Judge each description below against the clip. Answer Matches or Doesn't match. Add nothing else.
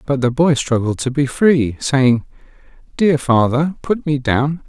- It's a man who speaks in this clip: Matches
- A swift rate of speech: Doesn't match